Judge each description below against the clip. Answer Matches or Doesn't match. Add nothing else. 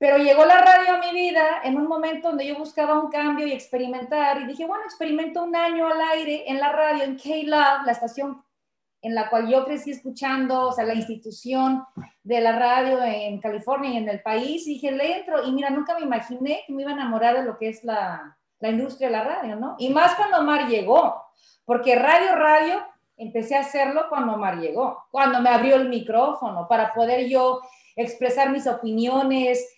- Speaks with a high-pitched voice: Matches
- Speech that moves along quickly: Matches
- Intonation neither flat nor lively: Matches